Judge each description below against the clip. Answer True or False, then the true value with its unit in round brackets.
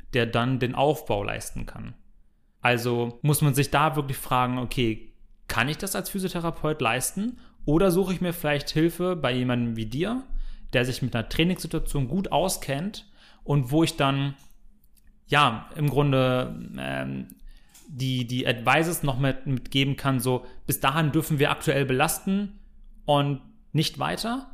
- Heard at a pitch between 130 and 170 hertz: True (140 Hz)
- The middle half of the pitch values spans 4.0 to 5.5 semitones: True (4.6 semitones)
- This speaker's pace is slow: False (150 wpm)